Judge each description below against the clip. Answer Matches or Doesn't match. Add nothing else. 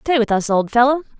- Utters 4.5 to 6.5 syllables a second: Matches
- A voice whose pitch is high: Matches